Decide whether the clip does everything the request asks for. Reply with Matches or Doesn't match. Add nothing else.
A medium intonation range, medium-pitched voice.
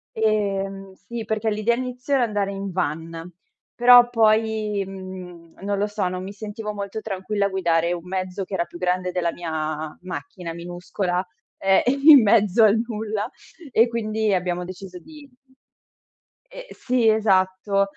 Doesn't match